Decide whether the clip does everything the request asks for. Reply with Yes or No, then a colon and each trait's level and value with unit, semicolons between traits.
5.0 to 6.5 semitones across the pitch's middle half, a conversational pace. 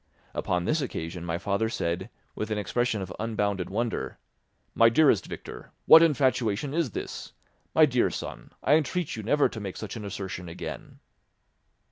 Yes: wide, 5.4 semitones; average, 160 wpm